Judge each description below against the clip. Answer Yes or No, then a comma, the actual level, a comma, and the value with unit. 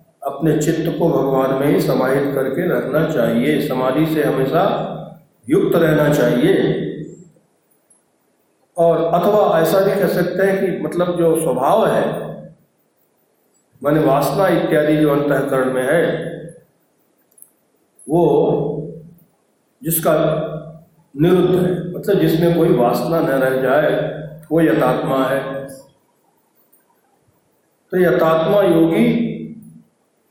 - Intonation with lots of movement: No, average, 3.8 semitones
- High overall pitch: No, medium, 160 Hz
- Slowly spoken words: Yes, slow, 105 wpm